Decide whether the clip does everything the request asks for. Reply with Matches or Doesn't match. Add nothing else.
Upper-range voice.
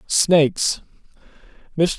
Doesn't match